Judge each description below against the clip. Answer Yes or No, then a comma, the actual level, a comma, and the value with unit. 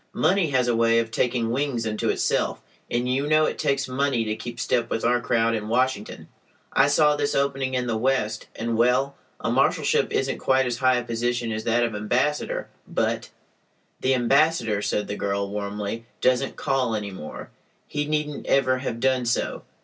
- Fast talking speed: No, average, 180 wpm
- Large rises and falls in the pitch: No, average, 2.9 semitones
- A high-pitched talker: No, low, 125 Hz